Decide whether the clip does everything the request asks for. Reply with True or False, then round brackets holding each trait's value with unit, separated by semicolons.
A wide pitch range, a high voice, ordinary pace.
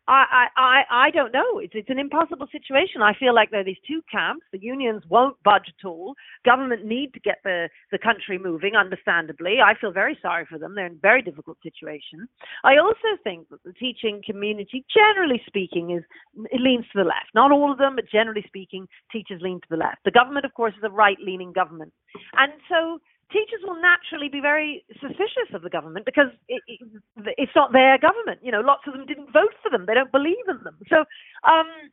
False (6.7 semitones; 235 Hz; 215 wpm)